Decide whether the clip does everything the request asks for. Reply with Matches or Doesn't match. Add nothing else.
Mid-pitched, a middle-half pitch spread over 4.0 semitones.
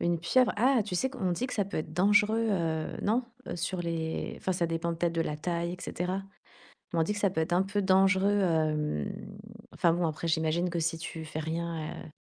Doesn't match